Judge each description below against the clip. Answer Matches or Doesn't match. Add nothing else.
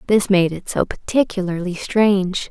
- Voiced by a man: Doesn't match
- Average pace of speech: Matches